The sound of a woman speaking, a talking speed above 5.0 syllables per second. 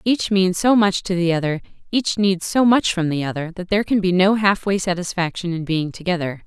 Yes: female; 5.5 syllables/s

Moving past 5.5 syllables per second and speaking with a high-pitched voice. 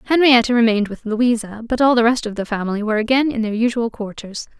Yes: 6.6 syllables/s; high, 230 Hz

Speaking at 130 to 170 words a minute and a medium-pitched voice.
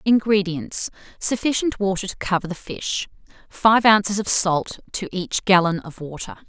No: average, 140 wpm; high, 195 Hz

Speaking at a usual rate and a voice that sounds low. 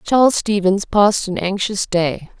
No: average, 150 wpm; high, 200 Hz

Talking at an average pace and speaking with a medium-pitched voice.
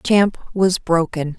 No: slow, 130 wpm; medium, 180 Hz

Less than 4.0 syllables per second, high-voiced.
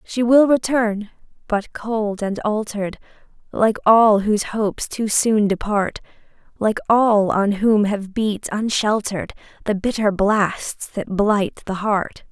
Yes: 3.7 syllables/s; high, 210 Hz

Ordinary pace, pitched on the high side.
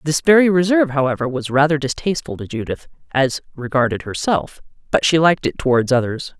No: average, 170 wpm; medium, 145 Hz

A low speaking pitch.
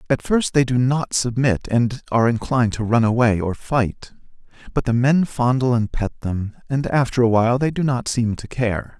Yes: low, 120 Hz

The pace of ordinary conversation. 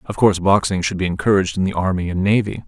No: fast, 245 wpm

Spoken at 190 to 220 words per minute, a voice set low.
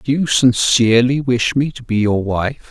Yes: average, 200 wpm; low, 125 Hz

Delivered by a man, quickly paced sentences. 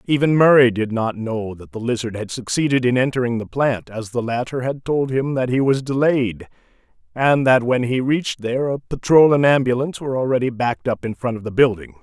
Yes: male; fast, 215 wpm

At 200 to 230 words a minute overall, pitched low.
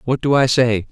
No: fast, 260 wpm; low, 125 Hz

